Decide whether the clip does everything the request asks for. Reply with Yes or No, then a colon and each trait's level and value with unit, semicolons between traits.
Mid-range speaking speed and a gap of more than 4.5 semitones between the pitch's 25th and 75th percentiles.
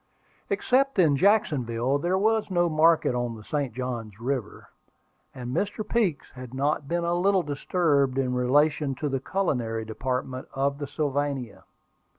Yes: average, 150 wpm; average, 5.2 semitones